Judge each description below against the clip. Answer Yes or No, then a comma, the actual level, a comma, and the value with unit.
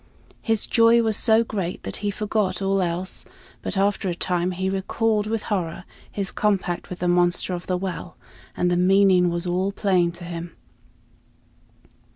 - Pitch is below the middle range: No, high, 190 Hz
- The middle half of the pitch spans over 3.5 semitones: No, narrow, 2.6 semitones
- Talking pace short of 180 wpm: Yes, average, 170 wpm